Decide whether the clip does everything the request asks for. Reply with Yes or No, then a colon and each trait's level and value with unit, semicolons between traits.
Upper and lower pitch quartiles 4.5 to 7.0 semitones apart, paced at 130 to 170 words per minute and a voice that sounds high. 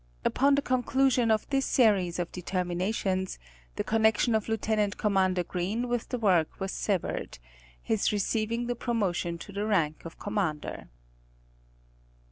No: average, 3.9 semitones; average, 140 wpm; high, 205 Hz